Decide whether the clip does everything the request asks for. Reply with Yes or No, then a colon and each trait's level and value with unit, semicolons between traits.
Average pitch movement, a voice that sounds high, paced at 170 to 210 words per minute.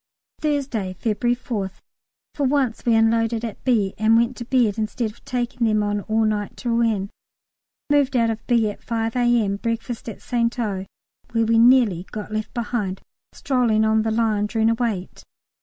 No: narrow, 2.0 semitones; high, 225 Hz; average, 175 wpm